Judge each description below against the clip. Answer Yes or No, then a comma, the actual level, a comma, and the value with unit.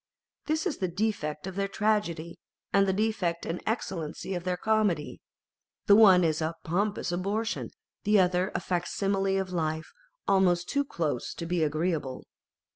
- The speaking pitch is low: No, medium, 185 Hz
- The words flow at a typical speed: Yes, average, 160 wpm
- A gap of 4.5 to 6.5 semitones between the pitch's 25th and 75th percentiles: No, average, 3.3 semitones